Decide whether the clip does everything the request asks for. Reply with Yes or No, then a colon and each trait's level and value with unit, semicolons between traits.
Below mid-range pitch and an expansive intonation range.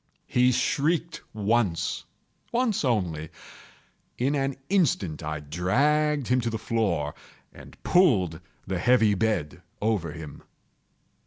Yes: low, 110 Hz; wide, 8.1 semitones